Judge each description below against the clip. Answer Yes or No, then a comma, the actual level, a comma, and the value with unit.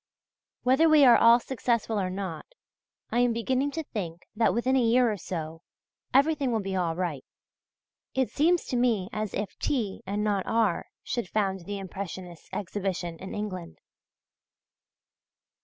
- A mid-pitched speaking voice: No, high, 210 Hz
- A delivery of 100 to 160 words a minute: Yes, average, 155 wpm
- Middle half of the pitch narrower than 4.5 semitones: No, average, 4.8 semitones